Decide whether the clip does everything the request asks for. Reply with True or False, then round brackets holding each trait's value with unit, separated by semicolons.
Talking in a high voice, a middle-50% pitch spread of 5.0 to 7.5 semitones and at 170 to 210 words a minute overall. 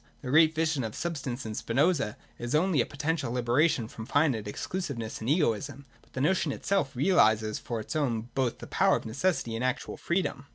False (135 Hz; 5.3 semitones; 195 wpm)